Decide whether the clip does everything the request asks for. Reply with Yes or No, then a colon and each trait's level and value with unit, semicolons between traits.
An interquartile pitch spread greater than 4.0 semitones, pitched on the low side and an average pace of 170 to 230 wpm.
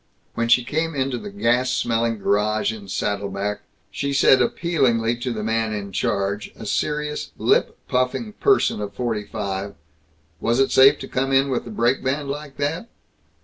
Yes: average, 4.5 semitones; low, 120 Hz; average, 175 wpm